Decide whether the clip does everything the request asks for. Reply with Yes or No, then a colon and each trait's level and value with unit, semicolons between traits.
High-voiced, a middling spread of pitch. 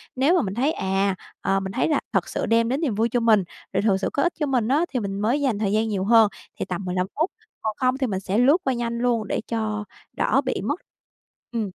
Yes: high, 225 Hz; average, 4.3 semitones